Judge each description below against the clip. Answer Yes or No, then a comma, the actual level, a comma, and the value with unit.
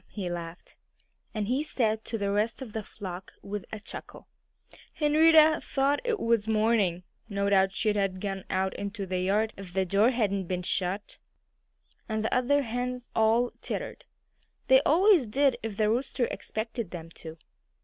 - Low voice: No, high, 215 Hz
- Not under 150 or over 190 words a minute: Yes, average, 165 wpm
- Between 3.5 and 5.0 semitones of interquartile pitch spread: Yes, average, 4.2 semitones